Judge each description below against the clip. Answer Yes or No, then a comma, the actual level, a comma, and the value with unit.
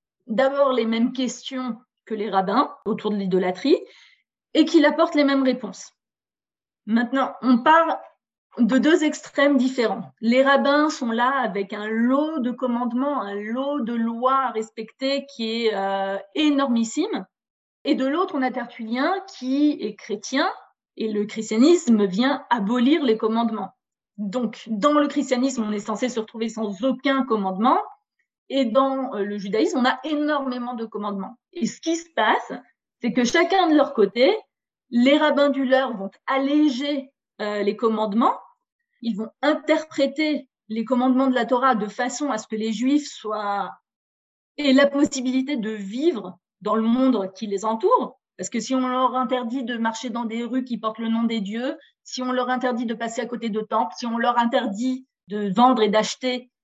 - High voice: Yes, very high, 250 Hz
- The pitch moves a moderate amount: Yes, average, 3.9 semitones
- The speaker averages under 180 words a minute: Yes, average, 170 wpm